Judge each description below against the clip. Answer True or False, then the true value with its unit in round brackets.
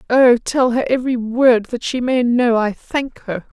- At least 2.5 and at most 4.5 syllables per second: True (4.2 syllables/s)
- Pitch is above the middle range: True (240 Hz)